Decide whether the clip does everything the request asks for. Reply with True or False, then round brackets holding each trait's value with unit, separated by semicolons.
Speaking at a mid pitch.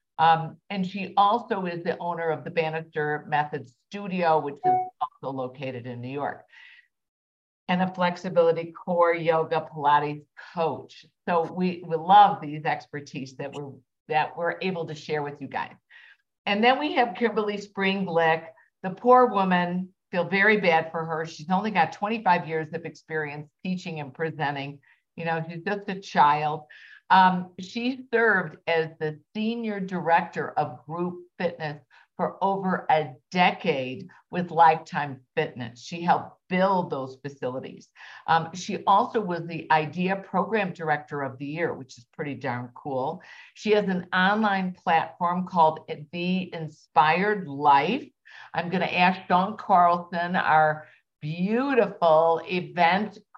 True (170 Hz)